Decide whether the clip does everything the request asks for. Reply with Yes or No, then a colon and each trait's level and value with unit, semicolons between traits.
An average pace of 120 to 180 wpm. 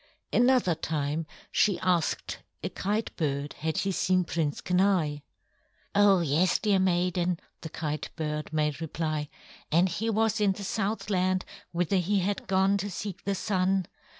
Yes: average, 150 wpm